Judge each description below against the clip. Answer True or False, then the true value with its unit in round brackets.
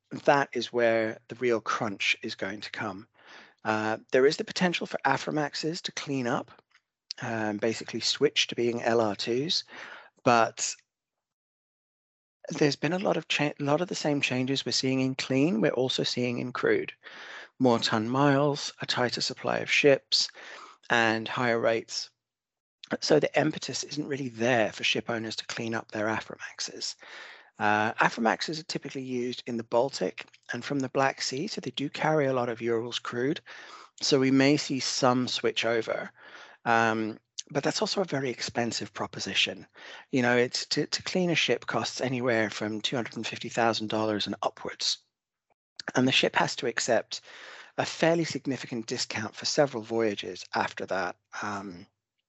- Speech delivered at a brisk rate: False (160 wpm)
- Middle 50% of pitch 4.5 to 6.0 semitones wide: False (3.9 semitones)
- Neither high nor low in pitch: False (125 Hz)